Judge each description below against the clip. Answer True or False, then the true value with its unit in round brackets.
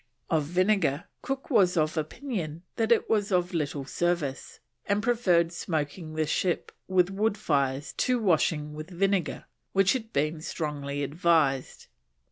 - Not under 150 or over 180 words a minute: False (140 wpm)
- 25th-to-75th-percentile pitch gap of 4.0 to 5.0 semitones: True (4.6 semitones)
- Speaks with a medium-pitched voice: True (170 Hz)